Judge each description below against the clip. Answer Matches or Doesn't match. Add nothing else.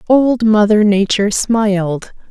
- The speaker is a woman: Matches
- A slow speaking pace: Matches